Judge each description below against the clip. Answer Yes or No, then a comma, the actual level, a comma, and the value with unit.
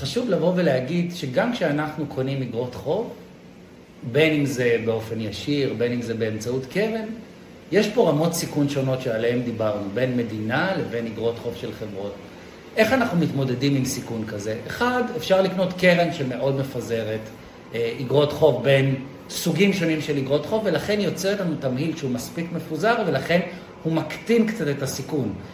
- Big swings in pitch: Yes, wide, 5.8 semitones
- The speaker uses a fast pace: Yes, fast, 155 wpm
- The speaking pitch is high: No, medium, 140 Hz